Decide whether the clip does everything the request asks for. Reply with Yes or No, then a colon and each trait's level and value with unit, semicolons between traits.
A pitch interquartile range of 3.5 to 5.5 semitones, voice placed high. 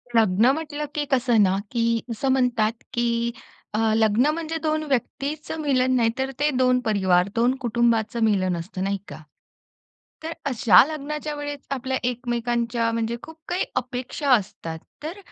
Yes: average, 4.0 semitones; high, 240 Hz